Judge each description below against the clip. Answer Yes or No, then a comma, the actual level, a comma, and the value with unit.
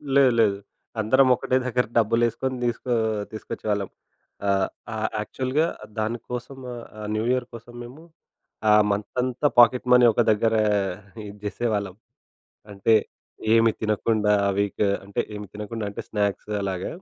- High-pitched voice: No, low, 110 Hz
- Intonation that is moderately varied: Yes, average, 3.0 semitones